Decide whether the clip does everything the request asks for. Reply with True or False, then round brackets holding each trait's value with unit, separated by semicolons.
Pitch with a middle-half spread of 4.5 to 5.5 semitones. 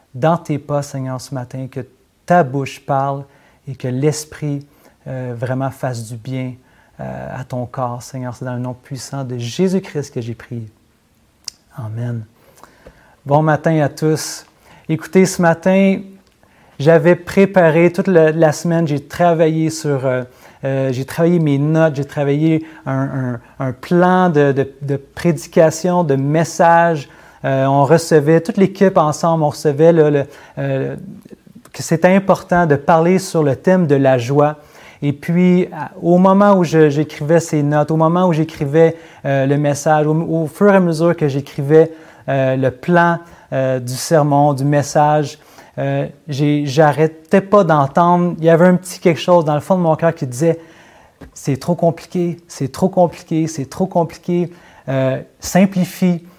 False (4.0 semitones)